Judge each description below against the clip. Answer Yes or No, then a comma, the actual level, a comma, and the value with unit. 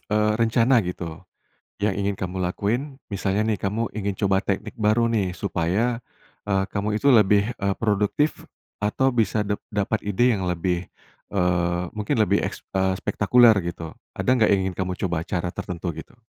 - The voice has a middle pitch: No, low, 100 Hz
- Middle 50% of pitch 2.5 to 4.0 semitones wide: Yes, average, 3.0 semitones